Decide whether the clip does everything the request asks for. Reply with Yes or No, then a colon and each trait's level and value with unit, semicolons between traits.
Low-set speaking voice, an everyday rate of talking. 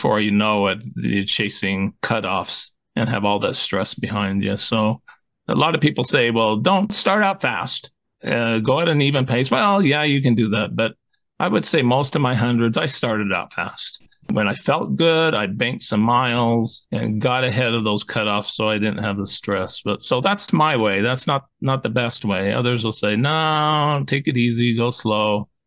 No: low, 120 Hz; fast, 210 wpm